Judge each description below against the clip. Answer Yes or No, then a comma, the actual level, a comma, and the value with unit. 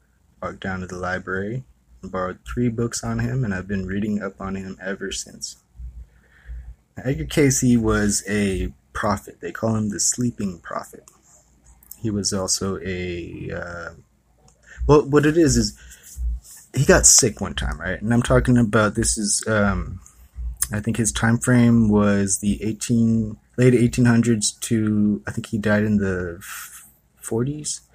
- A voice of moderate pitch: No, low, 105 Hz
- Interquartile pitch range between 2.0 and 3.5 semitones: No, average, 4.1 semitones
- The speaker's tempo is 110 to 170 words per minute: Yes, average, 160 wpm